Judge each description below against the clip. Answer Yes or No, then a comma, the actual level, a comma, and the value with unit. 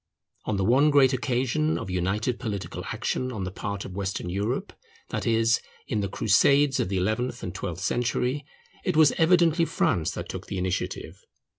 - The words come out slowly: No, average, 175 wpm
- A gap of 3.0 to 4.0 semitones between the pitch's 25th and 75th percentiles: No, wide, 5.5 semitones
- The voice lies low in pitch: Yes, low, 115 Hz